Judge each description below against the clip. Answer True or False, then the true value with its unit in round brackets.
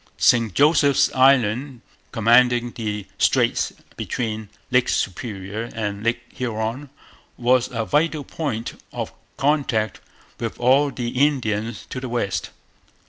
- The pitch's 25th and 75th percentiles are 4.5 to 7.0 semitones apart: False (3.1 semitones)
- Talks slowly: True (115 wpm)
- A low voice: True (120 Hz)